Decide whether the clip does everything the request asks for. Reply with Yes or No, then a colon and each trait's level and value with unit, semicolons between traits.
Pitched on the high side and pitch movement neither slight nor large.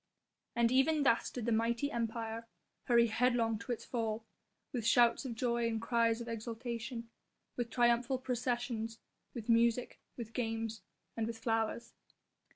No: high, 235 Hz; narrow, 1.2 semitones